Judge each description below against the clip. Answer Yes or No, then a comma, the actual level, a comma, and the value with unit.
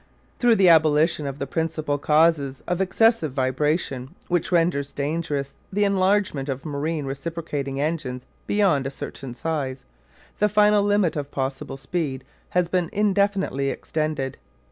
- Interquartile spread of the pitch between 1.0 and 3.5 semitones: No, average, 4.6 semitones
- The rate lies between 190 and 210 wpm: No, slow, 135 wpm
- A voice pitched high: No, medium, 155 Hz